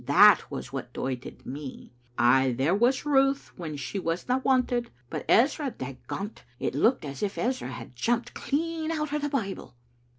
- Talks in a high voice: Yes, high, 230 Hz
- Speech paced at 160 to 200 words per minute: Yes, average, 165 wpm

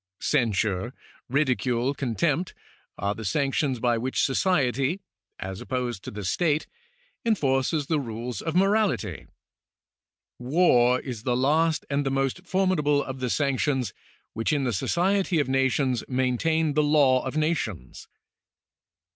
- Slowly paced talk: Yes, slow, 130 wpm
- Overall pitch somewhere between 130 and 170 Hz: Yes, low, 135 Hz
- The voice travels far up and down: No, average, 4.1 semitones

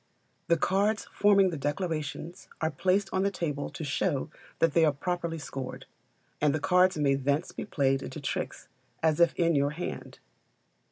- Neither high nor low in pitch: Yes, medium, 160 Hz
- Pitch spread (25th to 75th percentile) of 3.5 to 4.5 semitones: Yes, average, 3.9 semitones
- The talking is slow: No, average, 170 wpm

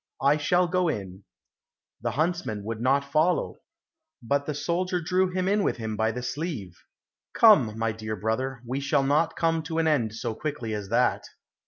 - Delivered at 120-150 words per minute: No, average, 180 wpm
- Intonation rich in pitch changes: Yes, wide, 6.7 semitones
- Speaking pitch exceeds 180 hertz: No, medium, 140 Hz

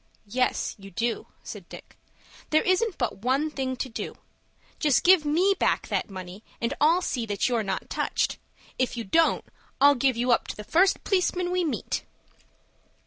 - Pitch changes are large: Yes, wide, 6.3 semitones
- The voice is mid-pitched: No, very high, 260 Hz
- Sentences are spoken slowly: No, average, 175 wpm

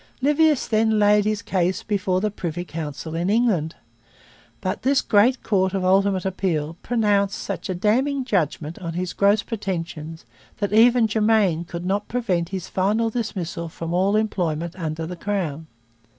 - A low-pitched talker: No, high, 195 Hz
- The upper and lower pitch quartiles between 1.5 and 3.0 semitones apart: No, average, 4.0 semitones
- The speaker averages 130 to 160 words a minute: Yes, average, 155 wpm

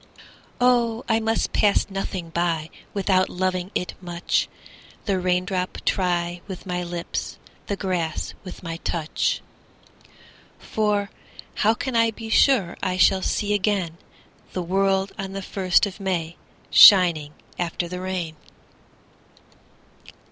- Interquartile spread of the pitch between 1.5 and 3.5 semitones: Yes, narrow, 2.5 semitones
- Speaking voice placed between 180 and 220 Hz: Yes, medium, 185 Hz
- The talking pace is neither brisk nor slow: No, slow, 125 wpm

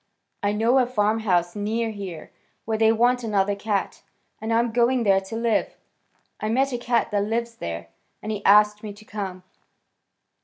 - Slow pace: No, average, 175 wpm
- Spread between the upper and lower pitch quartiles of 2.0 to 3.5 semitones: Yes, narrow, 2.4 semitones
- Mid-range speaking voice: No, high, 215 Hz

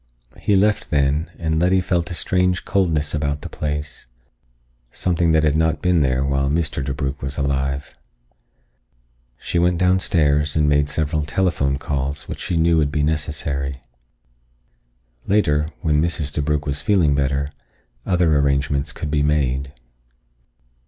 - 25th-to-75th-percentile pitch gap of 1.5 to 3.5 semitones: Yes, average, 3.0 semitones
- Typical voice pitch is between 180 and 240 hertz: No, very low, 75 Hz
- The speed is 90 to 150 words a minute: Yes, average, 140 wpm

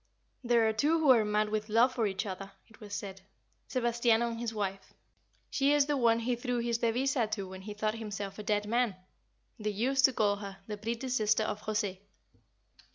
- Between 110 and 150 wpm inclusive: No, fast, 205 wpm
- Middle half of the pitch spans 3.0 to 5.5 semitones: No, narrow, 2.5 semitones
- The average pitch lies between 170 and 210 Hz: No, high, 220 Hz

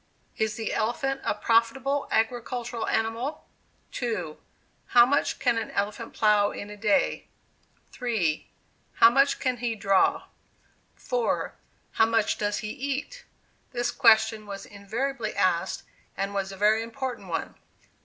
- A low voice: No, high, 225 Hz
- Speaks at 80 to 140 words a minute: Yes, slow, 135 wpm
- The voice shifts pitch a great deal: No, average, 3.3 semitones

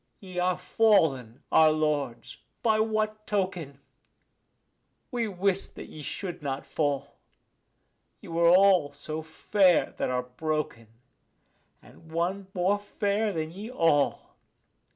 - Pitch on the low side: No, medium, 175 Hz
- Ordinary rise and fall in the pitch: Yes, average, 4.8 semitones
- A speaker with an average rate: No, slow, 120 wpm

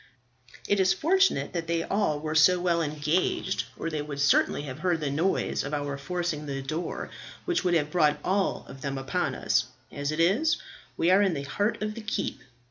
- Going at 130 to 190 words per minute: No, average, 200 wpm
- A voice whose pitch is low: No, medium, 165 Hz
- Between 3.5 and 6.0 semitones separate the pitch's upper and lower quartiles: Yes, average, 4.4 semitones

